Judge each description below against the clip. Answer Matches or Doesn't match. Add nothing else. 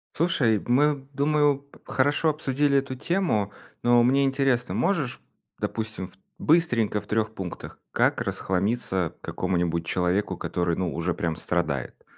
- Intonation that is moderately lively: Doesn't match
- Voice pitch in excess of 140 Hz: Doesn't match